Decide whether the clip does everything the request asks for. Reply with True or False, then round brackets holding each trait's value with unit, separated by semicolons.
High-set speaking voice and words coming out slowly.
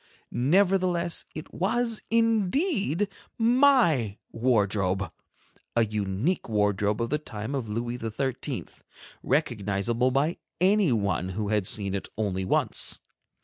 False (120 Hz; 105 wpm)